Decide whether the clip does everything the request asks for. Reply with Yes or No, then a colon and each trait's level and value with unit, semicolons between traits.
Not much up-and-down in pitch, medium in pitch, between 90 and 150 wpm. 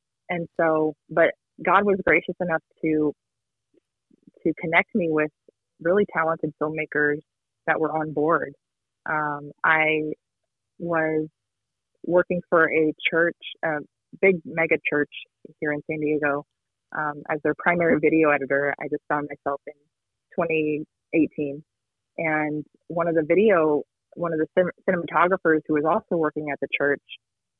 Yes: narrow, 2.1 semitones; medium, 155 Hz; slow, 135 wpm